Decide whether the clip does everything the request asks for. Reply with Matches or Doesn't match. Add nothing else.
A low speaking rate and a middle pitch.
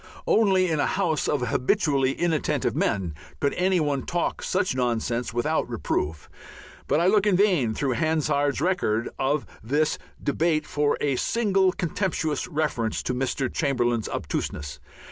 Doesn't match